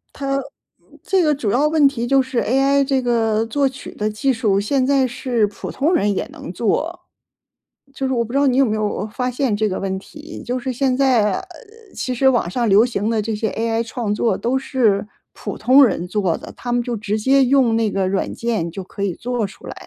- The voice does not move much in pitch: No, average, 4.1 semitones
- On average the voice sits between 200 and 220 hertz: No, high, 240 Hz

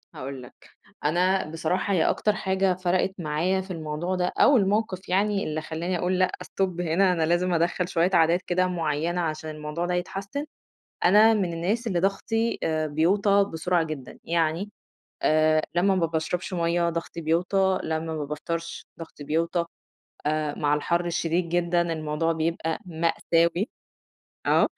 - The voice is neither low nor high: Yes, medium, 170 Hz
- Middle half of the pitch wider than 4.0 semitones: No, average, 2.7 semitones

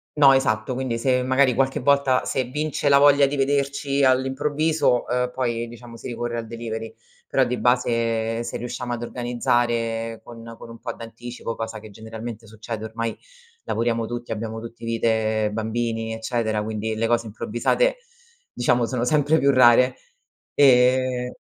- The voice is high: No, low, 120 Hz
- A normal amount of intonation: No, narrow, 2.3 semitones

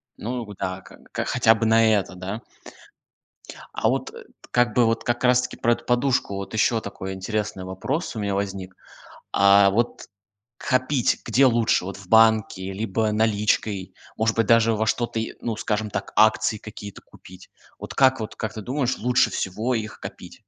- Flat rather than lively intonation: No, average, 3.0 semitones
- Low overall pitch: Yes, low, 110 Hz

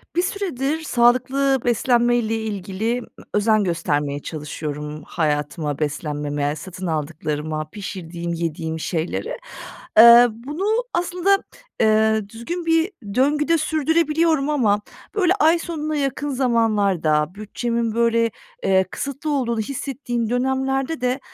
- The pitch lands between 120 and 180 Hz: No, high, 230 Hz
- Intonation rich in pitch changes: Yes, wide, 8.6 semitones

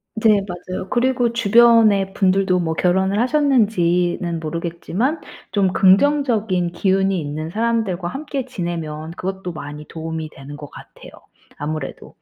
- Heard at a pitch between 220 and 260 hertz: No, high, 190 Hz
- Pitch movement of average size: Yes, average, 5.0 semitones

